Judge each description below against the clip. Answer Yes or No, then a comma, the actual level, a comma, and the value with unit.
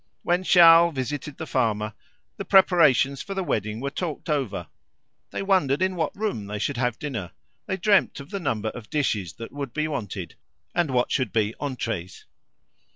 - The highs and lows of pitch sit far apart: Yes, wide, 7.4 semitones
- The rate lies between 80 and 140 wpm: No, average, 175 wpm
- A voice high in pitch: No, medium, 140 Hz